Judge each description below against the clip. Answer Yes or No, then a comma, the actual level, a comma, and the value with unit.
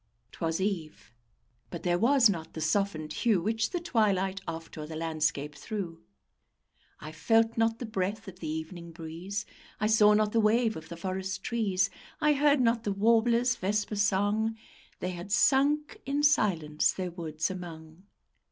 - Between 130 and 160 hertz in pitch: No, high, 195 Hz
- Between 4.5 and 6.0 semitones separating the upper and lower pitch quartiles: Yes, average, 5.2 semitones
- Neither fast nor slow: Yes, average, 160 wpm